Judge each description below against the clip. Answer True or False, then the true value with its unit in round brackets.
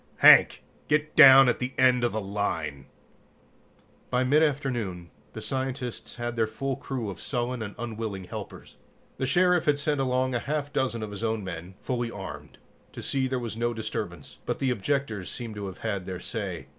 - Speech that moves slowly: False (185 wpm)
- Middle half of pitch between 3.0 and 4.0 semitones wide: False (4.4 semitones)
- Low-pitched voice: True (120 Hz)